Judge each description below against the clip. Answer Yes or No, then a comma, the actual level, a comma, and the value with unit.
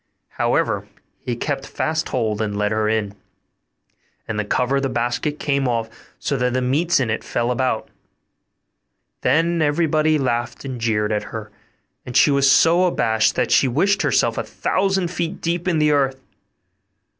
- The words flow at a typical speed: Yes, average, 170 wpm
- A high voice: No, low, 130 Hz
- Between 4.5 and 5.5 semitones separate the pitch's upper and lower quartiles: Yes, average, 5.2 semitones